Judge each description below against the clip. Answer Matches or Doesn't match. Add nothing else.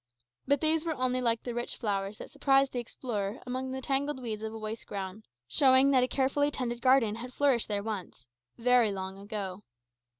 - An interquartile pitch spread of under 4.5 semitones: Matches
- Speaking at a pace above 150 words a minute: Matches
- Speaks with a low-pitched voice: Doesn't match